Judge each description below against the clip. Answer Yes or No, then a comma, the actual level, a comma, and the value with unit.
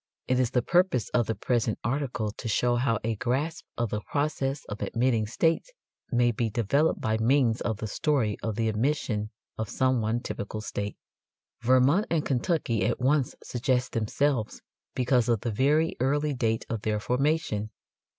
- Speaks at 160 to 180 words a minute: Yes, average, 170 wpm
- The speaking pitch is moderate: No, low, 120 Hz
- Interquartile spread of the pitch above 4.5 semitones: No, average, 3.7 semitones